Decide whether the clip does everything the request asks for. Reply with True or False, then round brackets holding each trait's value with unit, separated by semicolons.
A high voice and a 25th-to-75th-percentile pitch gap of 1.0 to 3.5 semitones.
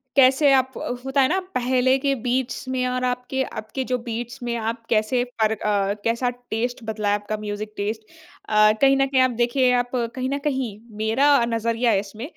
True (245 Hz; 3.0 semitones)